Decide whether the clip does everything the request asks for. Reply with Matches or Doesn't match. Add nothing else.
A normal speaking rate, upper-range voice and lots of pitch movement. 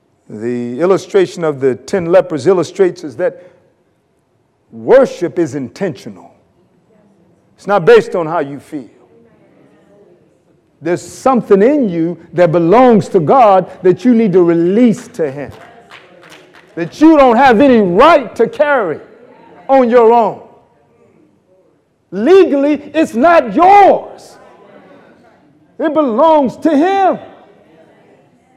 Doesn't match